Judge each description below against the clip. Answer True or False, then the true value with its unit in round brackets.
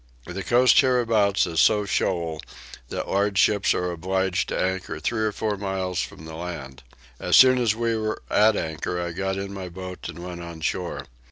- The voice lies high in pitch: False (95 Hz)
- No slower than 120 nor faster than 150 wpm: False (190 wpm)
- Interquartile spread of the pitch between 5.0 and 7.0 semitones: False (3.3 semitones)